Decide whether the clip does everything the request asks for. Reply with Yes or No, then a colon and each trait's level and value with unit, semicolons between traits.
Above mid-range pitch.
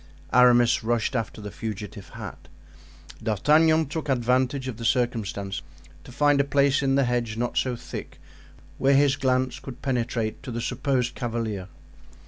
No: low, 125 Hz